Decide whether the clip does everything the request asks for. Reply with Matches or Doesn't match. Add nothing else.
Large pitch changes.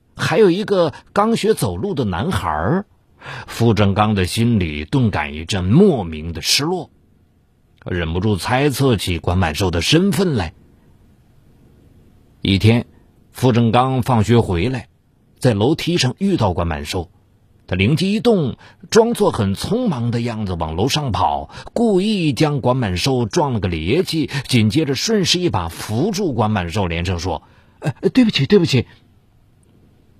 Matches